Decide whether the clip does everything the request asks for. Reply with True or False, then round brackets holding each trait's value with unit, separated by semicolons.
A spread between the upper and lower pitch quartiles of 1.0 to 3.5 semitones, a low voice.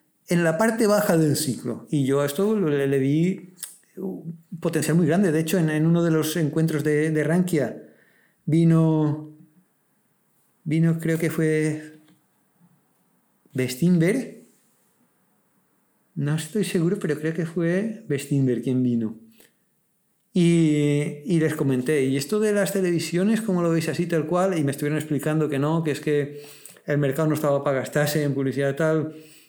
False (2.9 semitones; 155 Hz)